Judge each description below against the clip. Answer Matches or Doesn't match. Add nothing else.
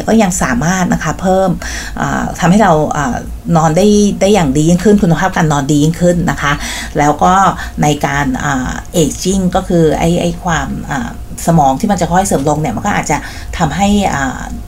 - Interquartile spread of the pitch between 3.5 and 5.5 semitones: Doesn't match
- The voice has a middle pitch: Matches